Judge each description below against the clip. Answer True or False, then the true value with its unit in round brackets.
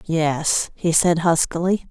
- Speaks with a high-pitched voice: False (165 Hz)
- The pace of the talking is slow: True (125 wpm)